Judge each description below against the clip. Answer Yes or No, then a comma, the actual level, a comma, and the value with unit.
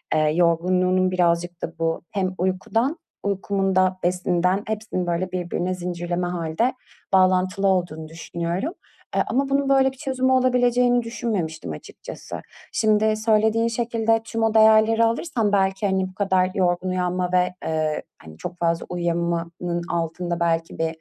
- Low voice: No, medium, 185 Hz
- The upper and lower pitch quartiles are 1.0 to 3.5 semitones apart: No, average, 4.1 semitones